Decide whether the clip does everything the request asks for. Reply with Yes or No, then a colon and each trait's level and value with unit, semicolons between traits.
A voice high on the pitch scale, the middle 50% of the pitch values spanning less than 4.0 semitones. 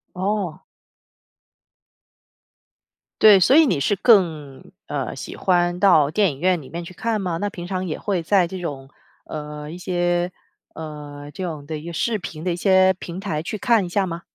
No: medium, 175 Hz; average, 3.5 semitones